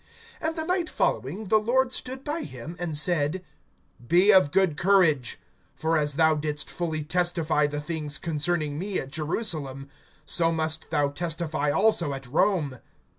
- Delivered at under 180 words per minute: Yes, average, 155 wpm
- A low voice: No, medium, 160 Hz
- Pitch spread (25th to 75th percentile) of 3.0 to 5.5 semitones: Yes, average, 4.2 semitones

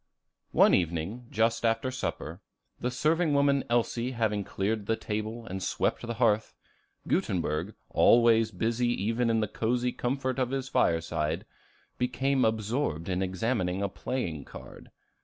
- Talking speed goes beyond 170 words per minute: No, average, 140 wpm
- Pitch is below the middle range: Yes, low, 115 Hz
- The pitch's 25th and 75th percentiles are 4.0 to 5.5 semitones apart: Yes, average, 4.3 semitones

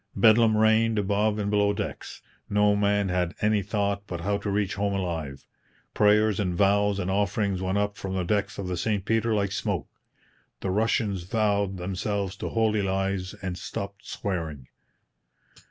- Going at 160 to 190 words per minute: Yes, average, 165 wpm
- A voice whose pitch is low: Yes, low, 100 Hz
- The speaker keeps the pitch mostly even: Yes, narrow, 1.7 semitones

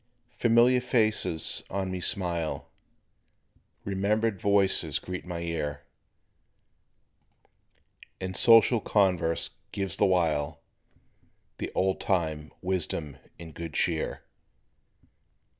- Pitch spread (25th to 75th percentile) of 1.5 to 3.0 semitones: No, average, 3.6 semitones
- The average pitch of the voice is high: No, very low, 95 Hz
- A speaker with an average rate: No, slow, 90 wpm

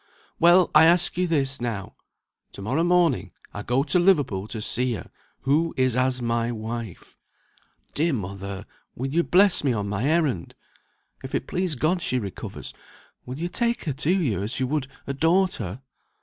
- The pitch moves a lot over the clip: Yes, wide, 6.8 semitones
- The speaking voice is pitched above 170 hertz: No, low, 135 Hz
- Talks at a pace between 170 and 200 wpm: Yes, average, 175 wpm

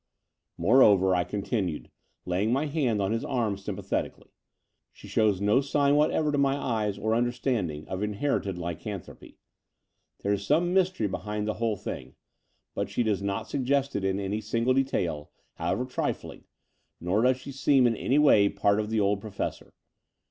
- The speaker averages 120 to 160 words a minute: No, average, 170 wpm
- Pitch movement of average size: Yes, average, 4.7 semitones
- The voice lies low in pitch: Yes, low, 110 Hz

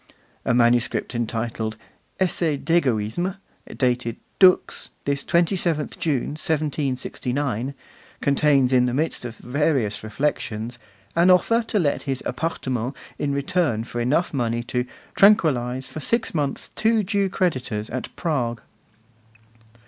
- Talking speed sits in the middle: No, slow, 120 wpm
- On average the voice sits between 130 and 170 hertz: Yes, medium, 140 Hz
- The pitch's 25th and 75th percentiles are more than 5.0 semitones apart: Yes, wide, 5.4 semitones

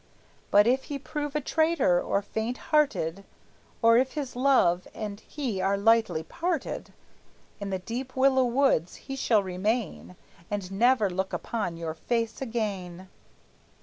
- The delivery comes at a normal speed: Yes, average, 145 wpm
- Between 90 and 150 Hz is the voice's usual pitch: No, high, 225 Hz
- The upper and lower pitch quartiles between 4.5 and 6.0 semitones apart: Yes, wide, 5.6 semitones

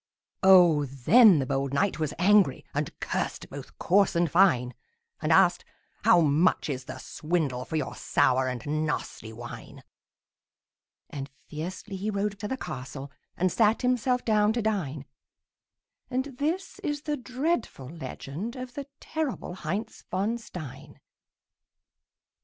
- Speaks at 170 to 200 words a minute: No, slow, 135 wpm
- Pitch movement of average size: No, wide, 8.2 semitones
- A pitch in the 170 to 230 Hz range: Yes, medium, 185 Hz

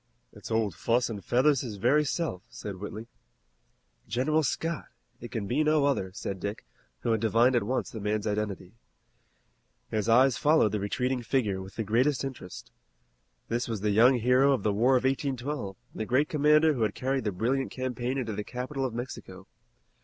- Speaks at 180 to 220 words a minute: Yes, average, 185 wpm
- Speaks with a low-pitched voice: Yes, low, 120 Hz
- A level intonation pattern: No, average, 4.1 semitones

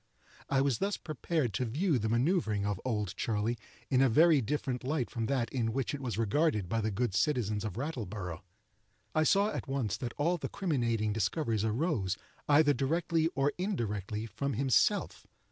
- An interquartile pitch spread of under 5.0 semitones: No, wide, 5.5 semitones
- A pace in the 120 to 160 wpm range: No, average, 175 wpm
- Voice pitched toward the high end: No, low, 125 Hz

